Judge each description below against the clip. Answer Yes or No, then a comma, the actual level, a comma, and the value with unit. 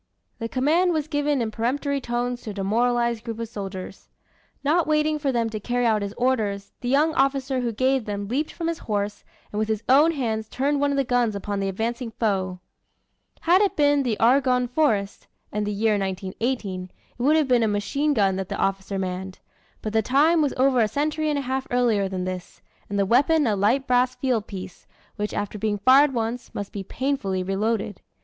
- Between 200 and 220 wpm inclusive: Yes, fast, 205 wpm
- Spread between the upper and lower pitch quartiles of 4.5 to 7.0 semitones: Yes, average, 5.1 semitones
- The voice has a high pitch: Yes, high, 235 Hz